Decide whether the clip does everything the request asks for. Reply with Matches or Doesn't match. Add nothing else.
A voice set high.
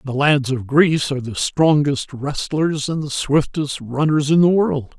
Doesn't match